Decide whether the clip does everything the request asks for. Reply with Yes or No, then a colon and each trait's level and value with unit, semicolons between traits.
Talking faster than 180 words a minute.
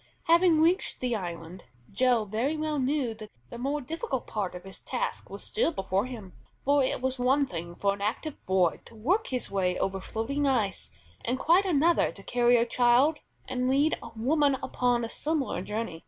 Yes: average, 190 wpm